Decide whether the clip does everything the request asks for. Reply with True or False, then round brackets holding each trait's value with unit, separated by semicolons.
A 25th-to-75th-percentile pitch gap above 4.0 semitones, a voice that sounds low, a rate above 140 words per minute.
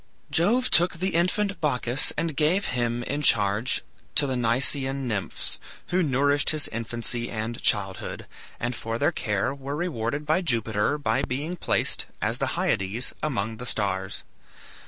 True (5.1 semitones; 130 Hz; 150 wpm)